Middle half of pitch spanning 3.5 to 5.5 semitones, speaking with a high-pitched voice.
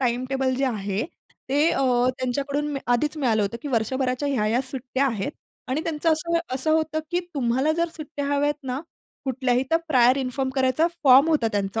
No: average, 3.0 semitones; very high, 265 Hz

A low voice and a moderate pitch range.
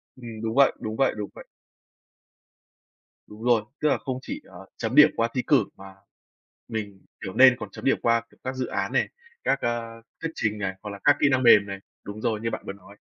Yes: low, 115 Hz; average, 3.8 semitones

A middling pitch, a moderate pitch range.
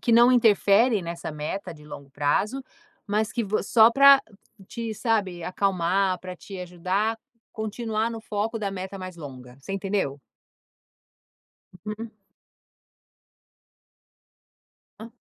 No: high, 200 Hz; average, 3.8 semitones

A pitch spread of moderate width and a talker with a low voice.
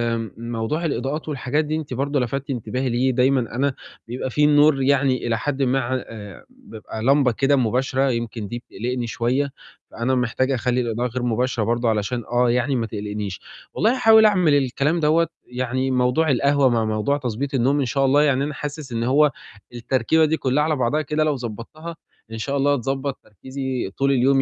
Yes: average, 3.1 semitones; low, 130 Hz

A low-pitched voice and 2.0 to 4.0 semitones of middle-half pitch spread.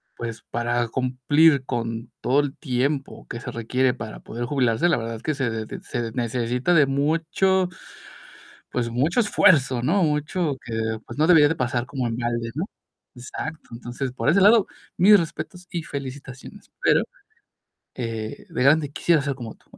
No: low, 130 Hz; average, 4.5 semitones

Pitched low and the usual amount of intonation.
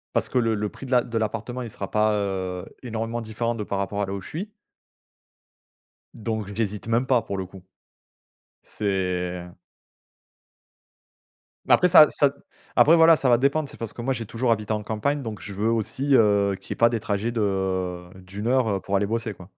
Yes: low, 110 Hz; average, 3.1 semitones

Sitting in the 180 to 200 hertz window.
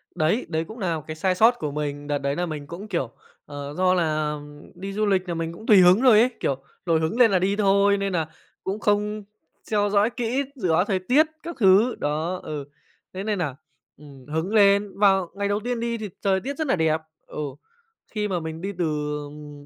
Yes: high, 190 Hz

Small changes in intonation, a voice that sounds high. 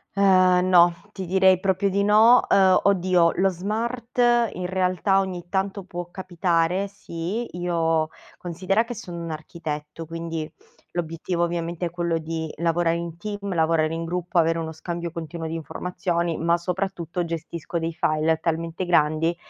No: narrow, 2.3 semitones; medium, 175 Hz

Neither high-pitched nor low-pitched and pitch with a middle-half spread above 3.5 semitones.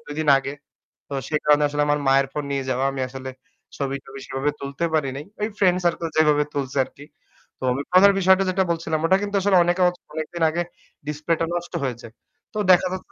Yes: medium, 150 Hz; average, 4.0 semitones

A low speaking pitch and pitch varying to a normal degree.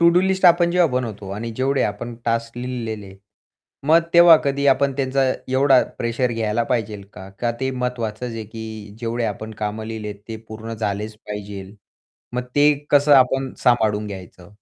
Yes: low, 115 Hz; average, 3.8 semitones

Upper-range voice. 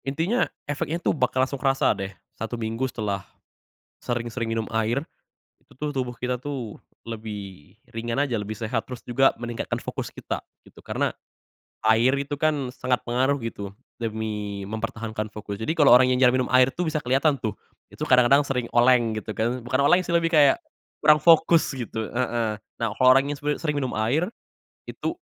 No: low, 125 Hz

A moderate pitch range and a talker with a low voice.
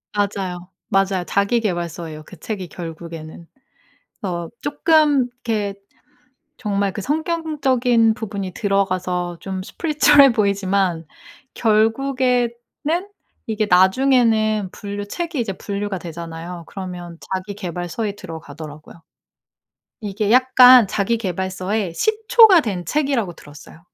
No: average, 5.0 semitones; high, 200 Hz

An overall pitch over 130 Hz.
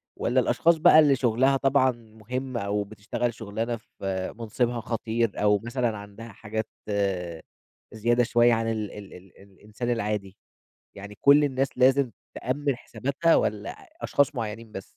No: low, 115 Hz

